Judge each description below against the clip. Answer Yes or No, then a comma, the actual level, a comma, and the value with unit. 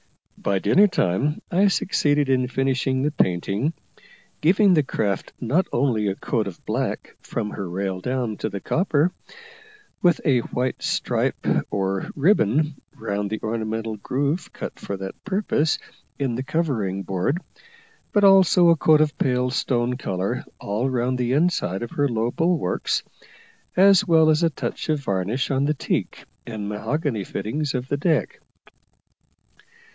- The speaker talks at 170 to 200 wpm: No, average, 150 wpm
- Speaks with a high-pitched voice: No, low, 130 Hz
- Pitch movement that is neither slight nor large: No, wide, 6.5 semitones